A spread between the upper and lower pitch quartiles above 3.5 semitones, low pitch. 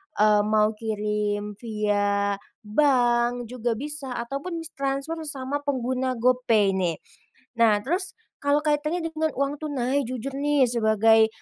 No: average, 4.9 semitones; high, 245 Hz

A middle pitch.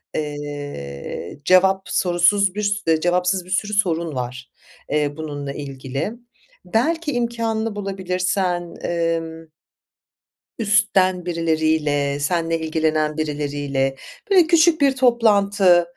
Yes: medium, 175 Hz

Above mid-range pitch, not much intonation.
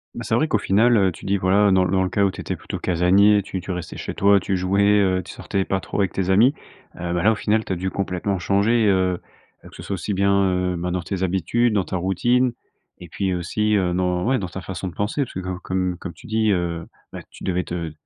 No: very low, 95 Hz; narrow, 2.0 semitones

